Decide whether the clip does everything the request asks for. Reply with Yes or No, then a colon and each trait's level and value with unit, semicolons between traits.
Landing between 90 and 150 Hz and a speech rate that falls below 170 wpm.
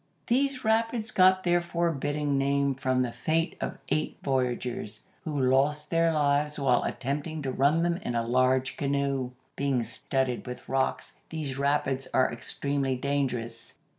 Yes: medium, 140 Hz; average, 145 wpm